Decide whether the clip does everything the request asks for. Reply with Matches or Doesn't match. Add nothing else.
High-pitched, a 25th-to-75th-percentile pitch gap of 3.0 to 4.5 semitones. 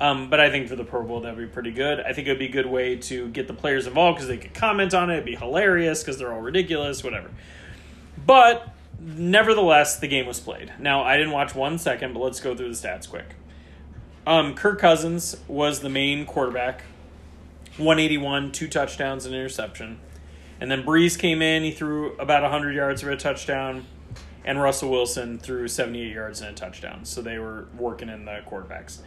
Doesn't match